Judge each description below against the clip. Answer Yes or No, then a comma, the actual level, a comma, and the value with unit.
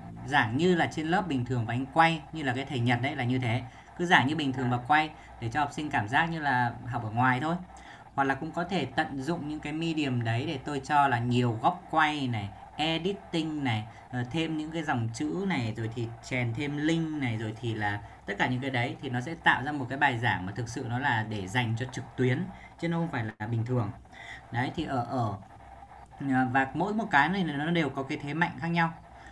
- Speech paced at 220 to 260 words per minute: Yes, fast, 250 wpm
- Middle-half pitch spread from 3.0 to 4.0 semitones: No, average, 4.5 semitones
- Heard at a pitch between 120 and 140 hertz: Yes, low, 135 Hz